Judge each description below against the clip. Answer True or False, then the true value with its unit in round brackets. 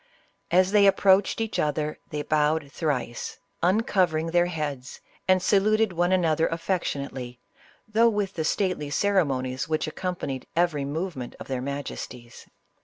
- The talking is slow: True (130 wpm)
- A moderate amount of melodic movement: True (4.8 semitones)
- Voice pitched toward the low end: False (165 Hz)